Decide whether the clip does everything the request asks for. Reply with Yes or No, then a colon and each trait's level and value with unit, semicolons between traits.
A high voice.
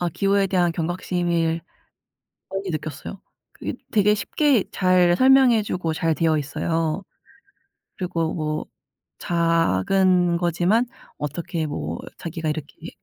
No: medium, 175 Hz